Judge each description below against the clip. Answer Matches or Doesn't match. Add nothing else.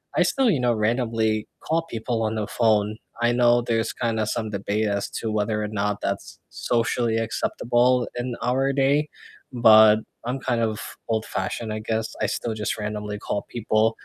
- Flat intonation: Matches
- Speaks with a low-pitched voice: Matches